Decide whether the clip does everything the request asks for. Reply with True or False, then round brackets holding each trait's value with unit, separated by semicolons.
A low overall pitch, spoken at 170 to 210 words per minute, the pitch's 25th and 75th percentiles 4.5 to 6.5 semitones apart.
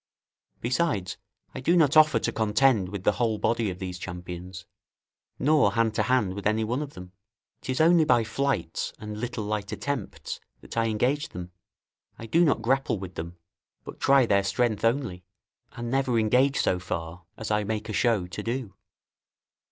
True (110 Hz; 175 wpm; 5.2 semitones)